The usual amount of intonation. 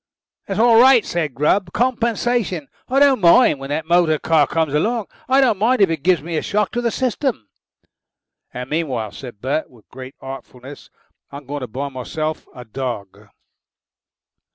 No: wide, 8.8 semitones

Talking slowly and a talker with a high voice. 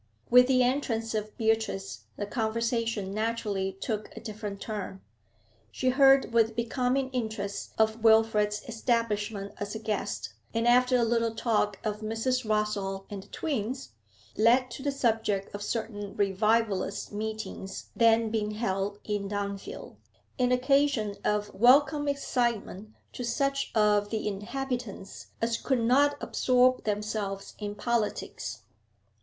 Yes: slow, 130 wpm; high, 220 Hz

